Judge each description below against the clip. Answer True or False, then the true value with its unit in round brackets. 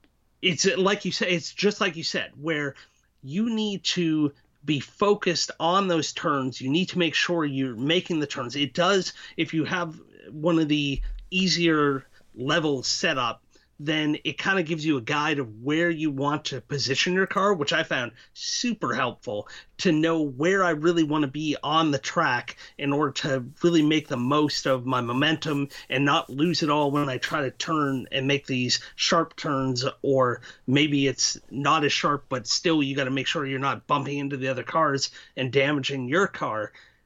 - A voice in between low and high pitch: True (150 Hz)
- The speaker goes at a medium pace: True (195 wpm)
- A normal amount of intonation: True (3.7 semitones)